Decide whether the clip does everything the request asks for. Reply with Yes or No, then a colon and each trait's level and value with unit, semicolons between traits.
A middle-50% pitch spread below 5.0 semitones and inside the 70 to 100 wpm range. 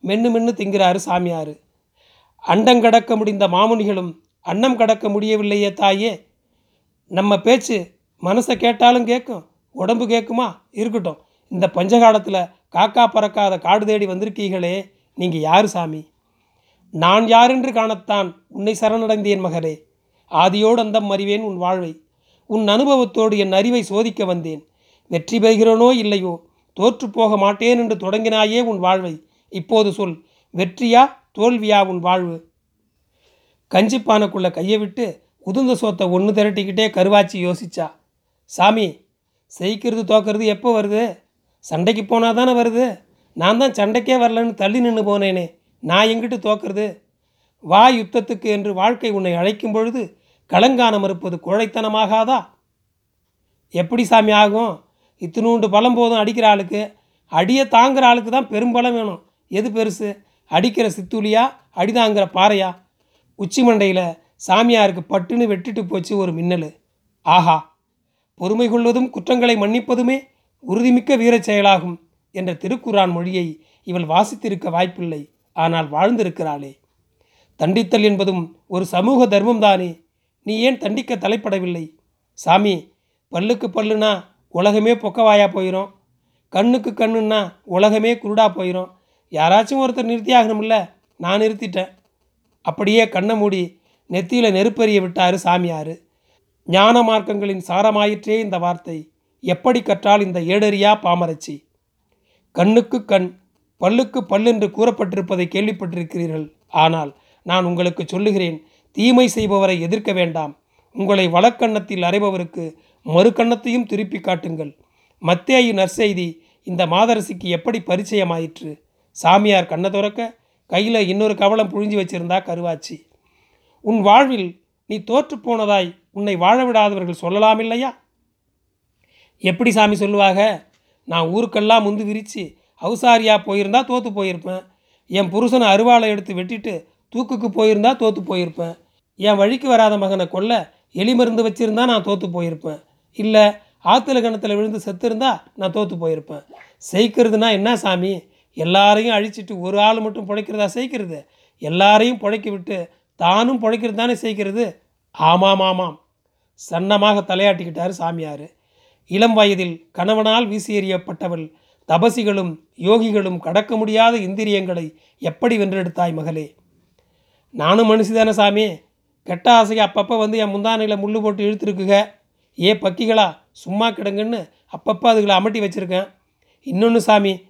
No: average, 3.8 semitones; average, 110 wpm